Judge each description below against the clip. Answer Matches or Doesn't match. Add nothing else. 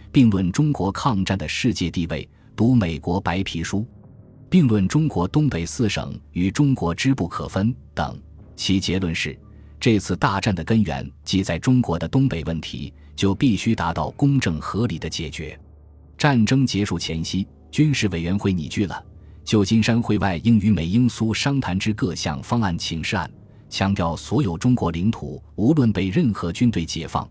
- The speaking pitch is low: Matches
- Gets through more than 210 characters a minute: Matches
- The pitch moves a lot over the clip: Matches